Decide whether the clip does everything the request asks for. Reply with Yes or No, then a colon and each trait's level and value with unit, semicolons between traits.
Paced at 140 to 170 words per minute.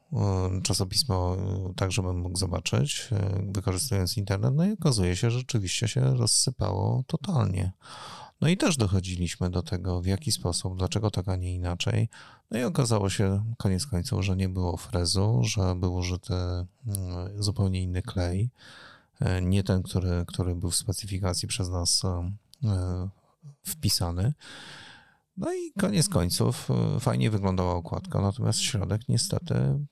No: average, 130 wpm